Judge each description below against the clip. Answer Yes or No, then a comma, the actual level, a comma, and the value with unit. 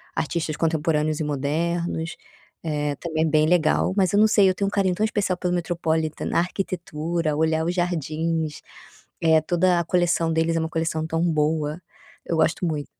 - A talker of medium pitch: Yes, medium, 165 Hz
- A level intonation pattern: Yes, narrow, 2.0 semitones